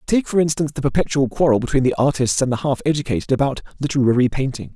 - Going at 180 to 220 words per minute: Yes, average, 200 wpm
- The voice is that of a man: Yes, male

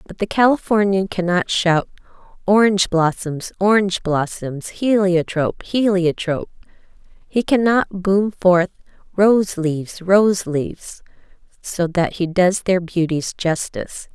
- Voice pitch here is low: No, medium, 185 Hz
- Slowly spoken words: Yes, slow, 100 wpm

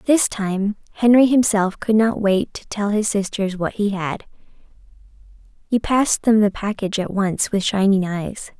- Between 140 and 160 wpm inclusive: No, average, 170 wpm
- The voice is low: No, high, 205 Hz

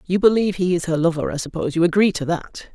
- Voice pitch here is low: No, medium, 175 Hz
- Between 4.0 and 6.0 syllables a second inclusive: No, 6.9 syllables/s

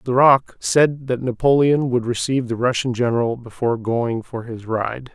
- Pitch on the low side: Yes, low, 125 Hz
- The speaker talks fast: No, average, 165 wpm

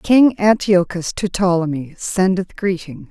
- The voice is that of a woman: Yes, female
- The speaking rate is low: Yes, slow, 115 wpm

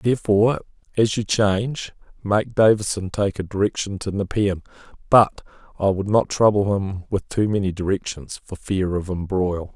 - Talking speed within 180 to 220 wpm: No, average, 155 wpm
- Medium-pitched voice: No, low, 100 Hz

